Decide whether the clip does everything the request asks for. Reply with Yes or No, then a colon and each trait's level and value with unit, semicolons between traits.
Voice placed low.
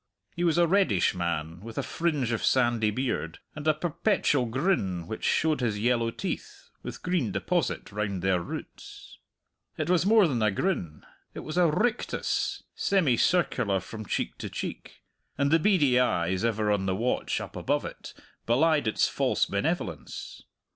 Yes: low, 125 Hz